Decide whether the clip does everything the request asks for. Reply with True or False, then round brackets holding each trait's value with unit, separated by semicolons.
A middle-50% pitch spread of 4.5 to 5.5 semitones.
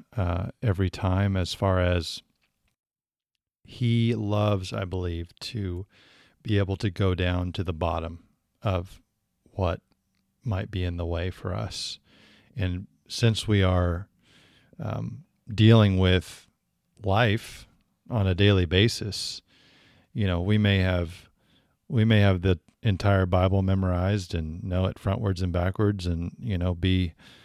False (2.5 semitones)